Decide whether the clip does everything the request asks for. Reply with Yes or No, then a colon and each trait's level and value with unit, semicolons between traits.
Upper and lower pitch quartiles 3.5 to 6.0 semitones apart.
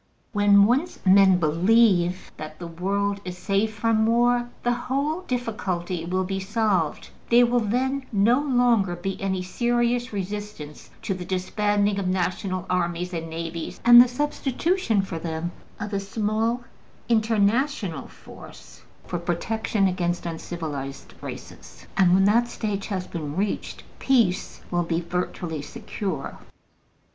Yes: average, 4.6 semitones